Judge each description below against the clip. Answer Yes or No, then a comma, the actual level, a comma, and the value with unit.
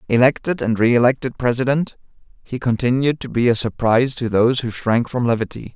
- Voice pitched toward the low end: Yes, low, 120 Hz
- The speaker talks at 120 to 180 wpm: Yes, average, 165 wpm